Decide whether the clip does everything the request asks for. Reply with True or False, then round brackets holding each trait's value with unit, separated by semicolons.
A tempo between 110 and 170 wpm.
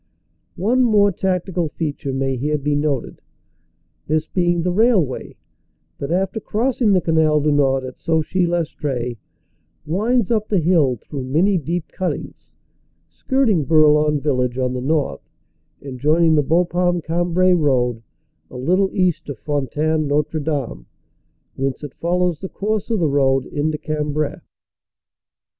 True (140 wpm)